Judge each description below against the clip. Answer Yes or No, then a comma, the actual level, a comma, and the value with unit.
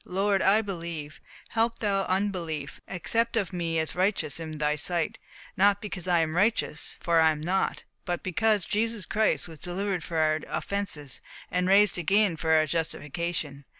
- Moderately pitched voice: Yes, medium, 180 Hz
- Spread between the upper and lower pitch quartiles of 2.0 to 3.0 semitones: No, average, 4.0 semitones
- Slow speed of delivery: No, average, 170 wpm